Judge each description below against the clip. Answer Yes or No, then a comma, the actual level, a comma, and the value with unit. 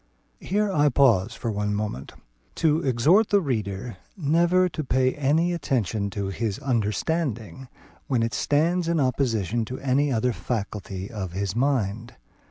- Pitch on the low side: Yes, low, 125 Hz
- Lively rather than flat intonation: Yes, wide, 6.0 semitones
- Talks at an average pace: Yes, average, 145 wpm